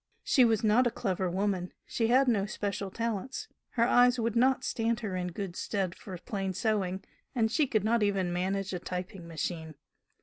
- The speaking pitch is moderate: No, high, 205 Hz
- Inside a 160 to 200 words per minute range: Yes, average, 190 wpm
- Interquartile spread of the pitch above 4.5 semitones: No, average, 3.9 semitones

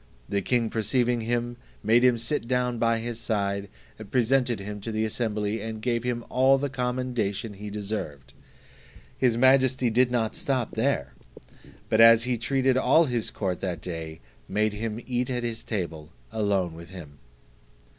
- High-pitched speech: No, low, 115 Hz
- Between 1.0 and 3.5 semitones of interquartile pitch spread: Yes, average, 3.2 semitones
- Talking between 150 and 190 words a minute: Yes, average, 160 wpm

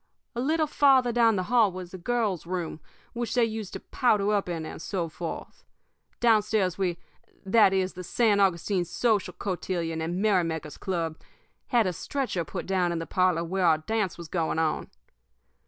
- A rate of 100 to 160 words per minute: No, average, 175 wpm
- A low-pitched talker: No, high, 190 Hz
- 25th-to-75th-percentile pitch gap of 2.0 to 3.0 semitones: No, average, 4.5 semitones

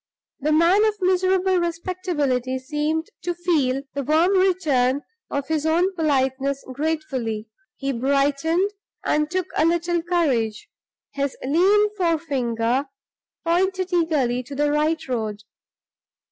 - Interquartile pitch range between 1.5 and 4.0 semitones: No, average, 4.6 semitones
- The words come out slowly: Yes, slow, 120 wpm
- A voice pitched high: Yes, very high, 310 Hz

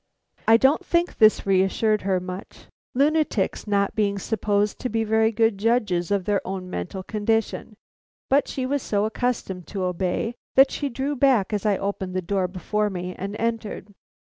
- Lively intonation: No, average, 3.2 semitones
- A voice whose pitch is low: No, high, 210 Hz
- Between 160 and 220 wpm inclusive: Yes, average, 170 wpm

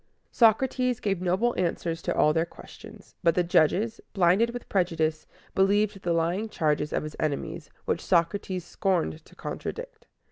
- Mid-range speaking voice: Yes, medium, 180 Hz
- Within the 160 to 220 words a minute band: No, average, 150 wpm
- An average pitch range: Yes, average, 4.2 semitones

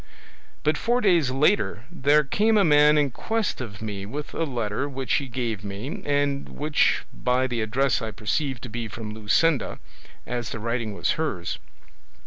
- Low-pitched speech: Yes, low, 130 Hz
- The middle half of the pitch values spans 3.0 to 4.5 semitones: No, average, 5.1 semitones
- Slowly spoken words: No, average, 170 wpm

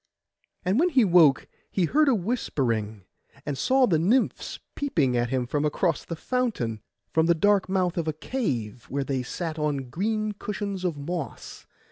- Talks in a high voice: No, medium, 170 Hz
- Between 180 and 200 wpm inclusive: No, average, 165 wpm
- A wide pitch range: Yes, wide, 7.3 semitones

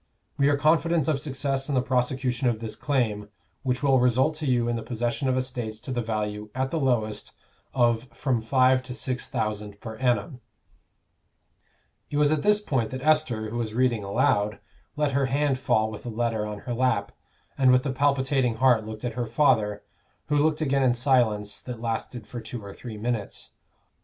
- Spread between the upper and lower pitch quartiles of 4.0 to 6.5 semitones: No, average, 3.3 semitones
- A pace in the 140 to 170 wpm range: No, average, 190 wpm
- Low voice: Yes, low, 125 Hz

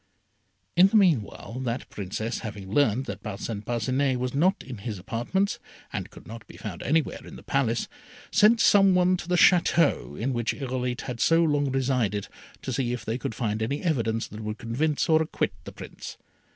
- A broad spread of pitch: Yes, wide, 5.8 semitones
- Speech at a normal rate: Yes, average, 190 wpm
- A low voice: Yes, low, 125 Hz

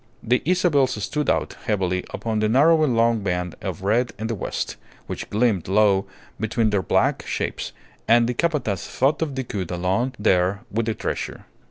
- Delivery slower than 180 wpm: Yes, average, 170 wpm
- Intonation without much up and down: No, average, 4.5 semitones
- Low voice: Yes, low, 110 Hz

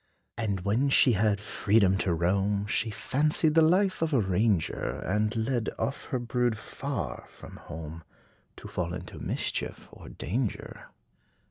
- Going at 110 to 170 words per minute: Yes, average, 145 wpm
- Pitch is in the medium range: No, low, 110 Hz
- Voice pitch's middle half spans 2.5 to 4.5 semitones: No, average, 5.1 semitones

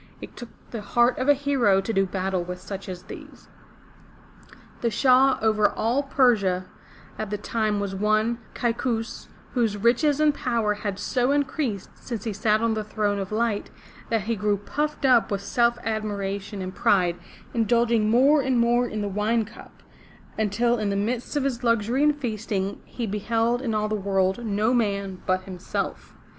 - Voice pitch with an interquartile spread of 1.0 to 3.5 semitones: Yes, average, 3.1 semitones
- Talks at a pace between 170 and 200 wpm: Yes, average, 175 wpm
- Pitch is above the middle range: Yes, high, 220 Hz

